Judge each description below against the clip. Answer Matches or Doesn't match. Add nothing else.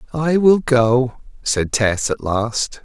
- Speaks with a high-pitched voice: Doesn't match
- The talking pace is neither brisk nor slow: Matches